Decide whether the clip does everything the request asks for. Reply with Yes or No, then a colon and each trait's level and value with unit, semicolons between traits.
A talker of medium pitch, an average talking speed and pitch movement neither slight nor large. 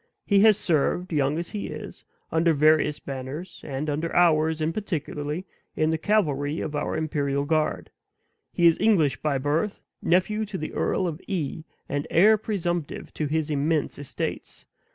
Yes: medium, 155 Hz; average, 160 wpm; average, 3.3 semitones